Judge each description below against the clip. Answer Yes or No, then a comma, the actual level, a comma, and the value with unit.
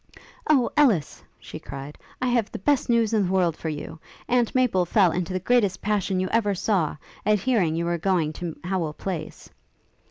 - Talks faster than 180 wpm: Yes, average, 190 wpm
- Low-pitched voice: No, high, 190 Hz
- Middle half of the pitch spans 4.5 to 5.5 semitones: Yes, average, 5.0 semitones